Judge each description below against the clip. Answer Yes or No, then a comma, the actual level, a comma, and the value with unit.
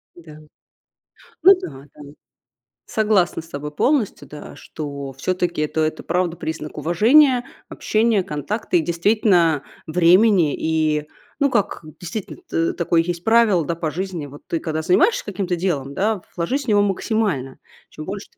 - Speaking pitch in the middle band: Yes, medium, 175 Hz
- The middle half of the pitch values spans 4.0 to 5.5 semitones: Yes, average, 5.0 semitones